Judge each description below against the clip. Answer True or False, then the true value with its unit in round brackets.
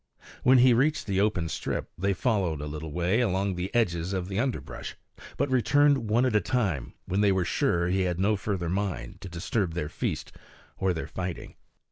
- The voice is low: True (95 Hz)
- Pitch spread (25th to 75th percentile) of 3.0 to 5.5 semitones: True (4.4 semitones)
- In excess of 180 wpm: True (195 wpm)